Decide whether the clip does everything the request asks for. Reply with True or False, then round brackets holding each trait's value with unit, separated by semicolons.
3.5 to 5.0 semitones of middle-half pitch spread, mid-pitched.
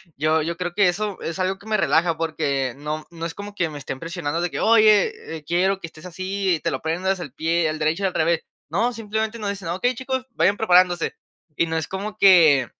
True (3.8 semitones; 175 Hz)